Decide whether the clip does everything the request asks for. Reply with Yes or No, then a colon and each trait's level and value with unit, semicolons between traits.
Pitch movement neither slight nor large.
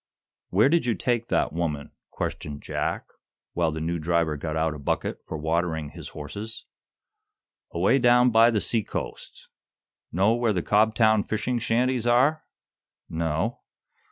No: wide, 6.7 semitones